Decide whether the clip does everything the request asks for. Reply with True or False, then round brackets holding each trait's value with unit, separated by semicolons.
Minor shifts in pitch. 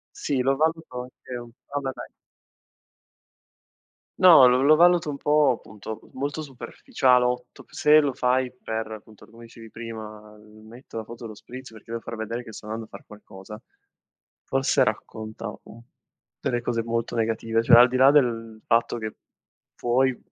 False (3.0 semitones)